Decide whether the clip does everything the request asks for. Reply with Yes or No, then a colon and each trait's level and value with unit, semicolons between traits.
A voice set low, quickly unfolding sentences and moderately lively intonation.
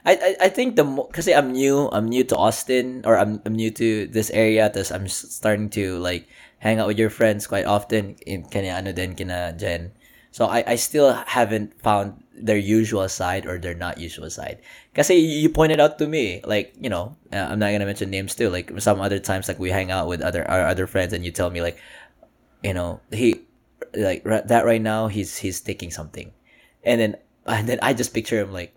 Yes: low, 105 Hz; fast, 210 wpm; average, 3.8 semitones